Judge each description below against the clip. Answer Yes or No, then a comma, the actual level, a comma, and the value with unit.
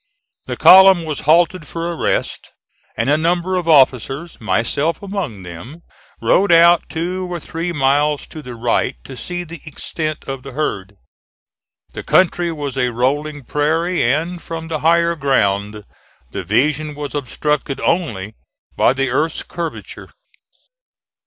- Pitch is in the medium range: Yes, medium, 150 Hz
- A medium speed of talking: Yes, average, 145 wpm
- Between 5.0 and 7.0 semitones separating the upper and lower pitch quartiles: No, average, 4.1 semitones